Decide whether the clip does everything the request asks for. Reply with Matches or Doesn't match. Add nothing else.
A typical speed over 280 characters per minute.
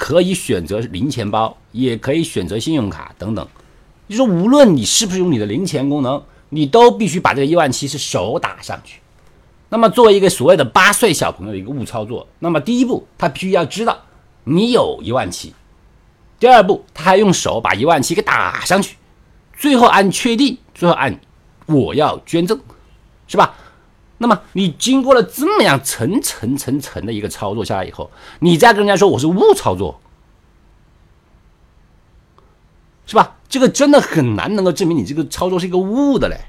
Doesn't match